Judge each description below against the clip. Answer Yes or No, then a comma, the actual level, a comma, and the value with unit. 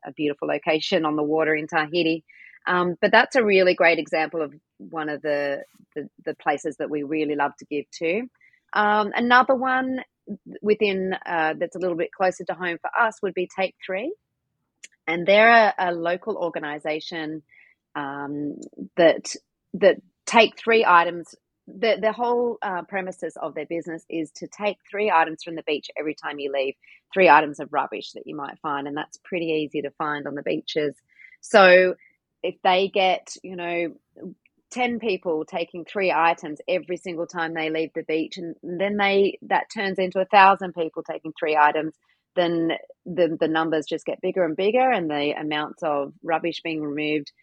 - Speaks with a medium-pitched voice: Yes, medium, 170 Hz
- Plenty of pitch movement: No, average, 3.9 semitones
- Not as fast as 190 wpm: Yes, average, 180 wpm